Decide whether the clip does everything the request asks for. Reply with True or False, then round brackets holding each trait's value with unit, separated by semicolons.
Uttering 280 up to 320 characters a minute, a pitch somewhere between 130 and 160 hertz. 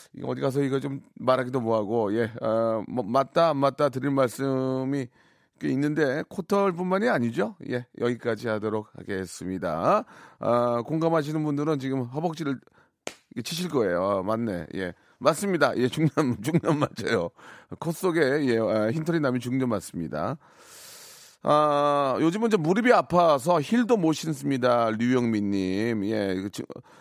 True (285 characters per minute; 135 Hz)